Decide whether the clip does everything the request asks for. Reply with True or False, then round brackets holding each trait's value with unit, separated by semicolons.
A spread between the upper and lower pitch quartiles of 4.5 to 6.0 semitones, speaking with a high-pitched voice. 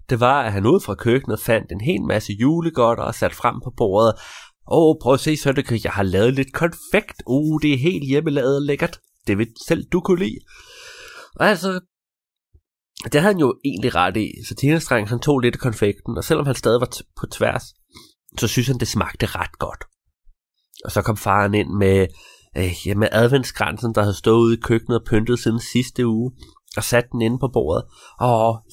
False (4.9 semitones; 120 Hz)